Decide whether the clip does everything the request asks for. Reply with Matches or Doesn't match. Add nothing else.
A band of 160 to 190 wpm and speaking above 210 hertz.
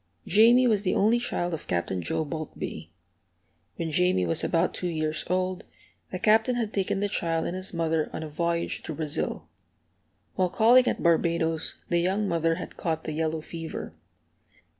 Doesn't match